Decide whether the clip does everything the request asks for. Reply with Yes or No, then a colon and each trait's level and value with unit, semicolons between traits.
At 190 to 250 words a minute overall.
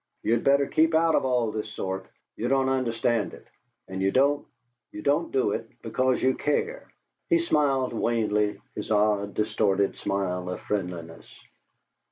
No: average, 155 wpm